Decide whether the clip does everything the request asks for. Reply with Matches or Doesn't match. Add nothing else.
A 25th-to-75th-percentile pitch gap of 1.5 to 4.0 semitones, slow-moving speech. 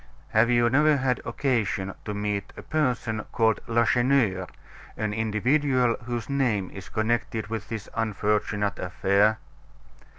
Matches